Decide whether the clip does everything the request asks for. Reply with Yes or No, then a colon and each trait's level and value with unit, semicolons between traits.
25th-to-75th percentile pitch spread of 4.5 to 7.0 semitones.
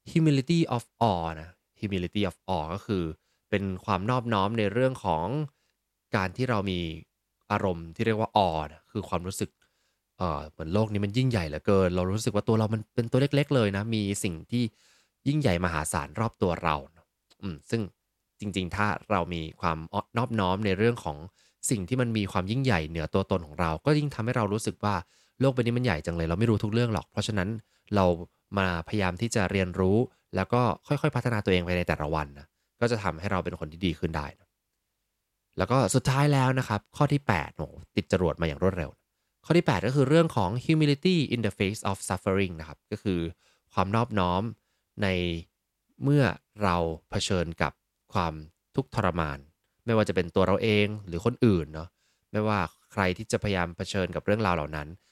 Yes: average, 4.8 semitones